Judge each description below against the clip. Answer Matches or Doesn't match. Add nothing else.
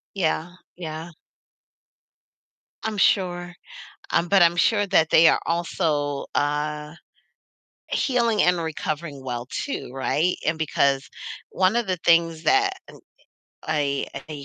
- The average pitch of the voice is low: Doesn't match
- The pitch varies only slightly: Doesn't match